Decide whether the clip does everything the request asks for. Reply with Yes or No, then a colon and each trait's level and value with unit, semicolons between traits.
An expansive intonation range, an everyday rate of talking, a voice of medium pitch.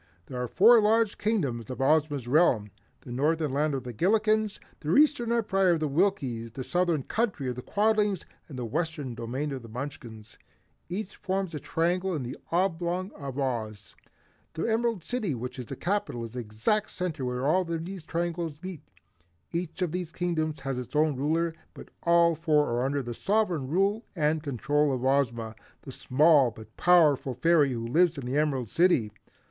Yes: wide, 5.9 semitones; average, 185 wpm; medium, 155 Hz